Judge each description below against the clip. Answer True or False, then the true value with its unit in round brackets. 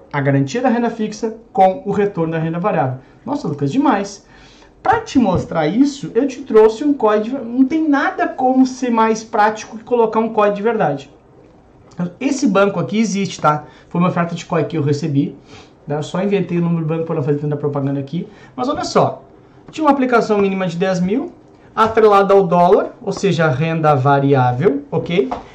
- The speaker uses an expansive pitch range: True (6.4 semitones)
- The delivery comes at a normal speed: False (190 wpm)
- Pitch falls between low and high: False (195 Hz)